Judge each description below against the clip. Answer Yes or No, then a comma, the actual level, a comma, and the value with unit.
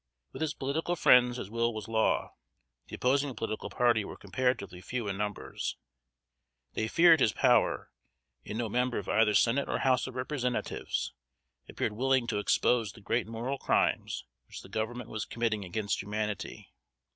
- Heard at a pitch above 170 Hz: No, low, 115 Hz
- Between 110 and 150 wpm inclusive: No, average, 160 wpm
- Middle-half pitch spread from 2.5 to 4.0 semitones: Yes, average, 3.1 semitones